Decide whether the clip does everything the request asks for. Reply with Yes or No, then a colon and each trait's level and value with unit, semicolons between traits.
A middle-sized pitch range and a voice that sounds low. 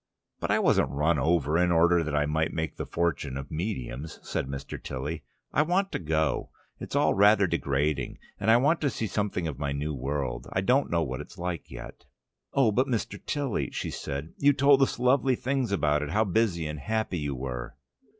No: wide, 7.4 semitones; very low, 85 Hz